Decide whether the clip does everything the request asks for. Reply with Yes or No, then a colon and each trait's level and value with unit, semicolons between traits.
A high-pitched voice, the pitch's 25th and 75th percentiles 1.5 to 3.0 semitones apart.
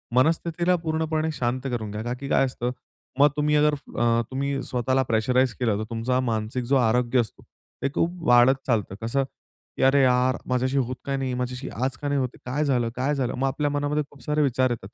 No: low, 130 Hz; narrow, 2.6 semitones